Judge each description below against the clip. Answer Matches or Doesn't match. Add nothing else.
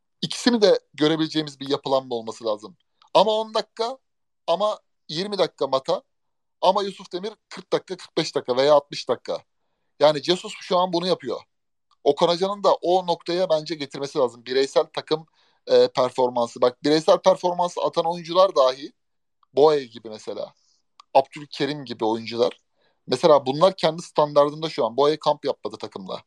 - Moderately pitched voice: Matches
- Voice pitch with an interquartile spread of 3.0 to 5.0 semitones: Matches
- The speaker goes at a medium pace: Doesn't match